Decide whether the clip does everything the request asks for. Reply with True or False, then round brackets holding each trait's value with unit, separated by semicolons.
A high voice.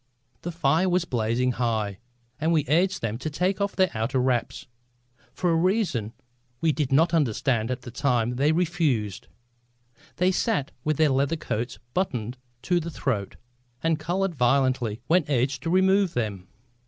False (140 Hz)